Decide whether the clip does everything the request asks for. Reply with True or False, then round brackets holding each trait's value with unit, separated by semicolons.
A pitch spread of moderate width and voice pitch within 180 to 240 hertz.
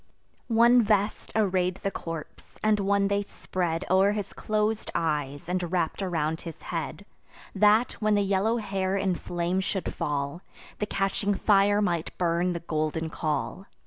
True (3.4 semitones; 190 Hz)